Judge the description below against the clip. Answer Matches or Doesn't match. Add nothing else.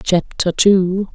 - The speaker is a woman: Matches